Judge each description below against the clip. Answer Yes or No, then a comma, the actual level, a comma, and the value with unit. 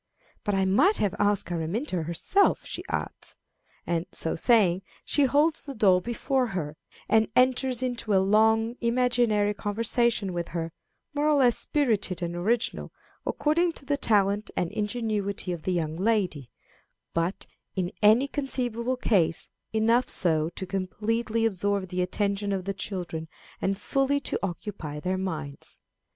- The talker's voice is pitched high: Yes, high, 205 Hz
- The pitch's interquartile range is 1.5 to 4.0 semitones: No, average, 4.8 semitones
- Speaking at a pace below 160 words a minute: Yes, average, 145 wpm